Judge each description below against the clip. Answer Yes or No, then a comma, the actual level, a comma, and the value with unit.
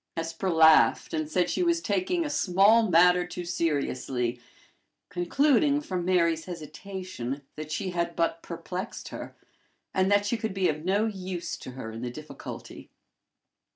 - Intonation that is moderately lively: Yes, average, 3.7 semitones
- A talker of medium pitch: Yes, medium, 180 Hz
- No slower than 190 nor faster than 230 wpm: No, average, 155 wpm